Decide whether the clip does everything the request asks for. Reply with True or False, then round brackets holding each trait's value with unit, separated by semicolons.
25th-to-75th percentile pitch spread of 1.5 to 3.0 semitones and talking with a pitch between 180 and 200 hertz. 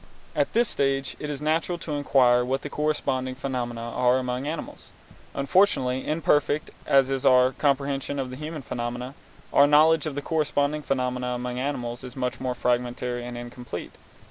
False (2.7 semitones; 135 Hz)